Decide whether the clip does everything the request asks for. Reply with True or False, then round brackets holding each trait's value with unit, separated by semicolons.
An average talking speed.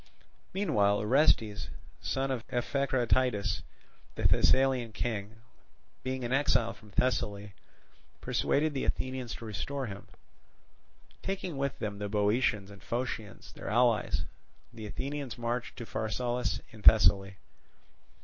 False (115 wpm)